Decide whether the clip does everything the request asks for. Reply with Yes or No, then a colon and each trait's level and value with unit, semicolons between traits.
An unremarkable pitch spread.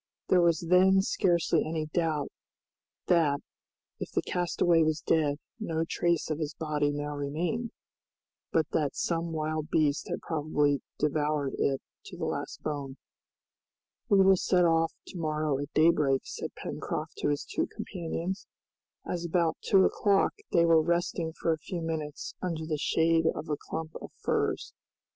No: narrow, 2.3 semitones